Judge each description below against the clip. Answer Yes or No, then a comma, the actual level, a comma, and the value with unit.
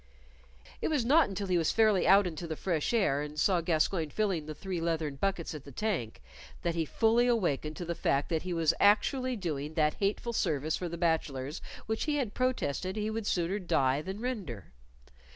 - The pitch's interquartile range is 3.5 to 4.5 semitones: No, wide, 5.5 semitones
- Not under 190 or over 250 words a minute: Yes, average, 200 wpm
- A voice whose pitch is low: No, medium, 175 Hz